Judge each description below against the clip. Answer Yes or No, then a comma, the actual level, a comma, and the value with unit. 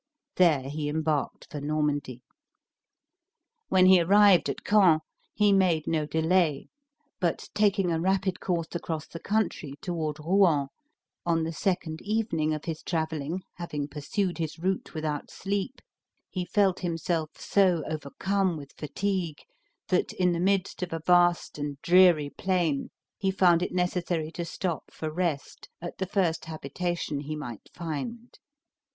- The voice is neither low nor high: Yes, medium, 170 Hz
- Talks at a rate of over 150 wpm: No, average, 145 wpm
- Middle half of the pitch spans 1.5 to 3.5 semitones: Yes, average, 3.2 semitones